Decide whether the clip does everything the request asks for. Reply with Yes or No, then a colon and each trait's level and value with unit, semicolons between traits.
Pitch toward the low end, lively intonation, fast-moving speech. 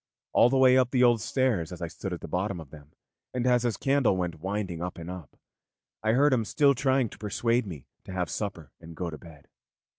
Yes: low, 100 Hz; wide, 6.6 semitones; fast, 235 wpm